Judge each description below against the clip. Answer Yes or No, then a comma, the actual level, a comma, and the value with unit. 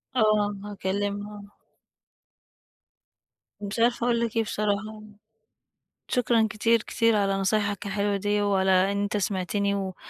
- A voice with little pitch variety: Yes, narrow, 1.4 semitones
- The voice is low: No, high, 205 Hz